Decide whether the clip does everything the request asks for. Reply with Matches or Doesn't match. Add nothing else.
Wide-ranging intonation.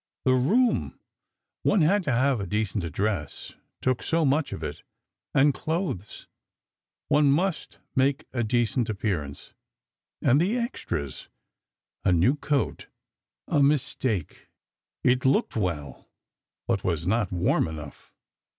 Matches